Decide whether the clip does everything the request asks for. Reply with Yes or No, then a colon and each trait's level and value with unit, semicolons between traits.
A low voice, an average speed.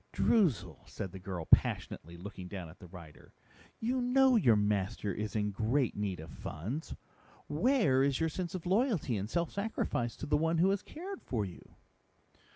Yes: low, 125 Hz; average, 175 wpm